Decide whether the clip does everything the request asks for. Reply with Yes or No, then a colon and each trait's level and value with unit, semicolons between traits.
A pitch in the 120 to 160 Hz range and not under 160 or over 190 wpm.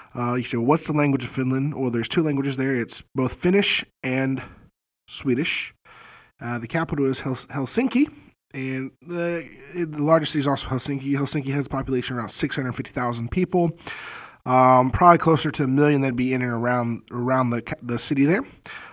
Yes: low, 135 Hz; average, 180 wpm